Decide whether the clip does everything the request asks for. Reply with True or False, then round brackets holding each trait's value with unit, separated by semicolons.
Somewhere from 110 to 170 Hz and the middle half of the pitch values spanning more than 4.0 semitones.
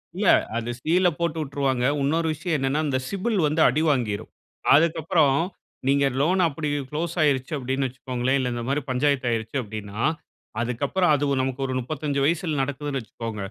False (140 Hz; 3.4 semitones)